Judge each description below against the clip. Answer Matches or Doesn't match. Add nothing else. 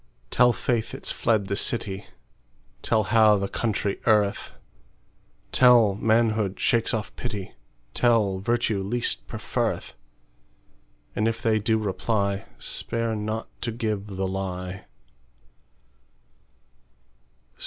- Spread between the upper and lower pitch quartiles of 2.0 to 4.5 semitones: Matches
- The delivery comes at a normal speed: Doesn't match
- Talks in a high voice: Doesn't match